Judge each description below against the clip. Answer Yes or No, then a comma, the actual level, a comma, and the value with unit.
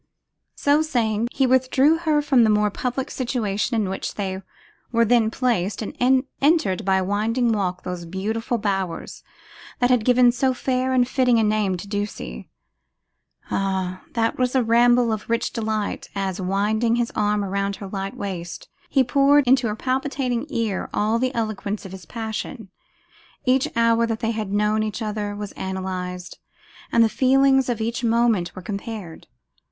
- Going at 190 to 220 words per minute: No, average, 165 wpm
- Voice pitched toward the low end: No, high, 220 Hz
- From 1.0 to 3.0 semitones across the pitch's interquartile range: No, average, 3.9 semitones